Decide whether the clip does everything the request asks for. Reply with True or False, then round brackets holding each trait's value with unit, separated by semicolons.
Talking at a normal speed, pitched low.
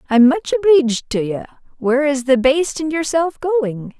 False (180 wpm; 285 Hz)